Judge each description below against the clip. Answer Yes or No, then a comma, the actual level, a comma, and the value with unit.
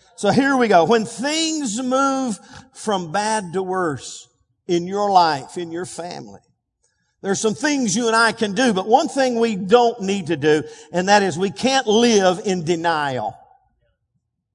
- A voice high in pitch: Yes, high, 210 Hz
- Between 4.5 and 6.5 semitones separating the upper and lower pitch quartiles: Yes, wide, 5.4 semitones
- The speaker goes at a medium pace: Yes, average, 170 wpm